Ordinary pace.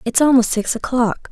Yes: average, 185 wpm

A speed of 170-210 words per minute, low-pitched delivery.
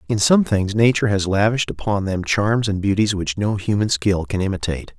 Yes: fast, 205 wpm; low, 100 Hz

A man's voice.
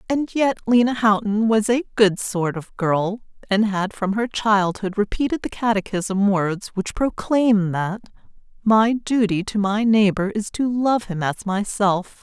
No: female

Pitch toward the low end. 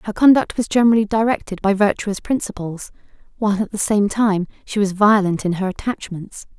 No: high, 205 Hz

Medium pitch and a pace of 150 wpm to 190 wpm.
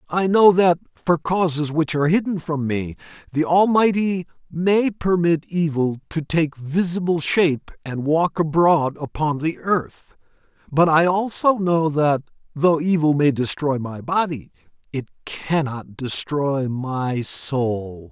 No: medium, 155 Hz; slow, 135 wpm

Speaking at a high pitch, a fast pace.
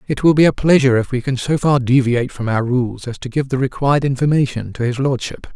No: low, 130 Hz; fast, 250 wpm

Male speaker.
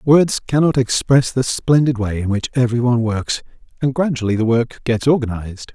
Yes: male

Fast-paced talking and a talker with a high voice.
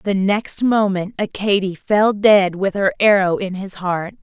No: average, 170 wpm; high, 195 Hz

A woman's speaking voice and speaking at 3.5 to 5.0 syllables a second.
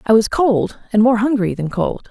Yes: female; 4.8 syllables/s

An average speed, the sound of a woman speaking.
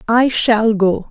Yes: average, 165 wpm; female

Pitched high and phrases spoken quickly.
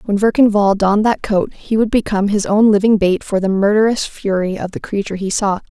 Yes: high, 205 Hz; fast, 230 wpm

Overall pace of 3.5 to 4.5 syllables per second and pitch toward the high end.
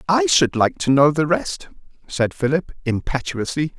No: 4.4 syllables/s; medium, 140 Hz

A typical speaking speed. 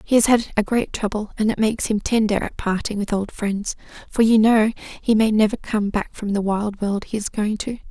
No: fast, 245 wpm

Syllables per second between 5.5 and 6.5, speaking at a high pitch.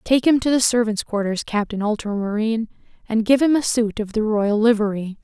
Yes: 5.6 syllables/s; high, 220 Hz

